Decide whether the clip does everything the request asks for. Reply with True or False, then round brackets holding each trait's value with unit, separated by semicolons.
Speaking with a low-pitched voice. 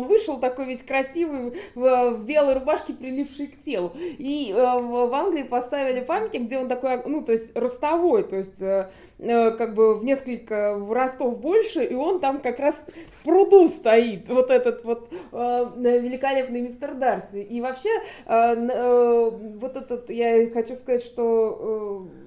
False (250 Hz)